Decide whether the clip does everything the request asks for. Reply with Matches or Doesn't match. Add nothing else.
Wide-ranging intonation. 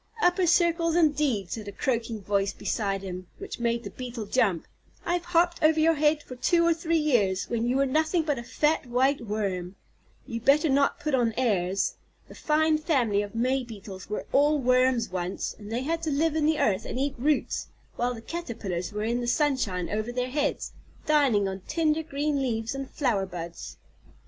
Matches